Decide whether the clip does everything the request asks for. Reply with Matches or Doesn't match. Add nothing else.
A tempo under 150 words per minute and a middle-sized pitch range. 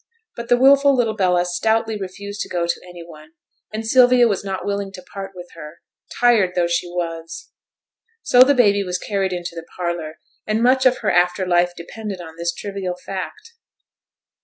Doesn't match